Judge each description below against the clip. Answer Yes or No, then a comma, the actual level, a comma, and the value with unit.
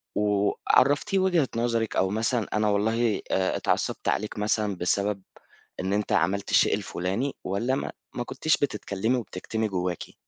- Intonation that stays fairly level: No, average, 3.4 semitones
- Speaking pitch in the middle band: No, low, 105 Hz